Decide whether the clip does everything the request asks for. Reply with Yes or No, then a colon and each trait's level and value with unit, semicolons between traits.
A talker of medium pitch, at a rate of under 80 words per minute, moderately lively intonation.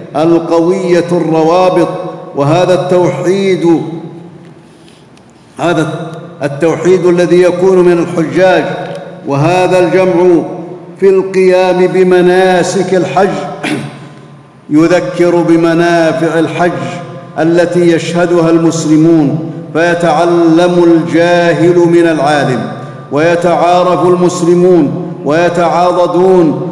No: medium, 175 Hz; slow, 65 wpm; narrow, 1.3 semitones